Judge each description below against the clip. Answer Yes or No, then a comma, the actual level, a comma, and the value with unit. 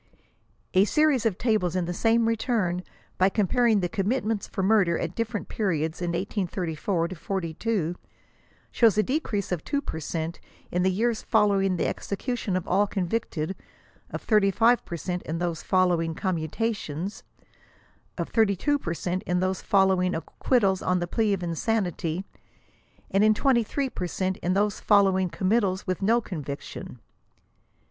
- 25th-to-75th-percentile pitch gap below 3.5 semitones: No, average, 3.8 semitones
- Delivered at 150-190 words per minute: Yes, average, 155 wpm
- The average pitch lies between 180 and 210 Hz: Yes, high, 190 Hz